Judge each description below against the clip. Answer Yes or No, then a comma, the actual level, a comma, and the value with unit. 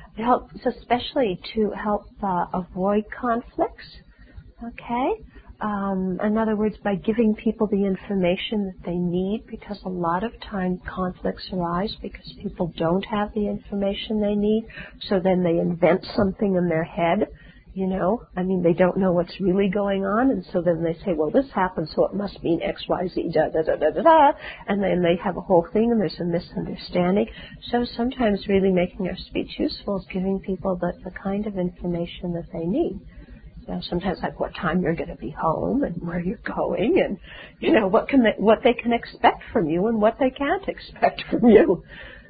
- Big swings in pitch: No, average, 3.3 semitones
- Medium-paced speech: Yes, average, 195 wpm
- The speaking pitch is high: Yes, high, 195 Hz